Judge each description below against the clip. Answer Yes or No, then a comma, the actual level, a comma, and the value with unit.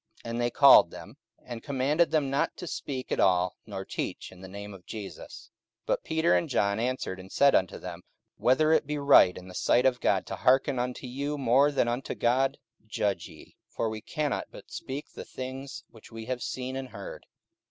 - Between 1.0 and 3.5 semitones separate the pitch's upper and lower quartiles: No, average, 4.5 semitones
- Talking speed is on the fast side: Yes, fast, 215 wpm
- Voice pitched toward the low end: Yes, low, 125 Hz